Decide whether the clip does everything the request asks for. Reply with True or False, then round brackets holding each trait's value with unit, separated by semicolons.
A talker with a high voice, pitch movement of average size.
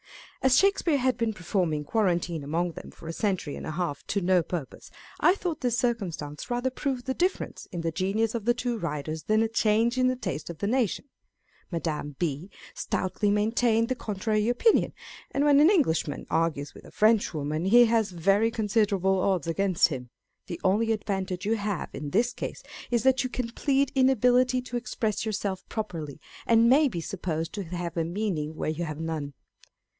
False (205 Hz; 6.2 semitones)